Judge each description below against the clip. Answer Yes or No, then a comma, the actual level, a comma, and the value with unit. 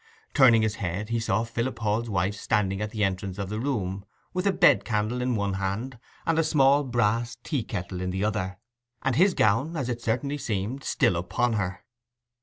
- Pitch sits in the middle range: No, low, 110 Hz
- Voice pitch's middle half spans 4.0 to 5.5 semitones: Yes, average, 4.4 semitones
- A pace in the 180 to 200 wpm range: Yes, average, 195 wpm